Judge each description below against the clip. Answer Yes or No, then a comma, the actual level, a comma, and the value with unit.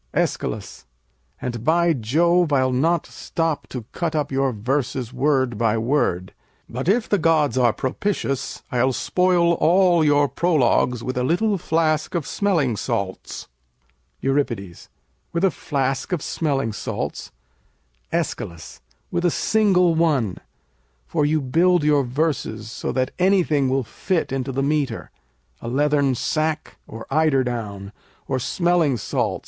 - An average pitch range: Yes, average, 4.9 semitones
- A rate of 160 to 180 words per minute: No, average, 140 wpm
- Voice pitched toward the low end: No, medium, 145 Hz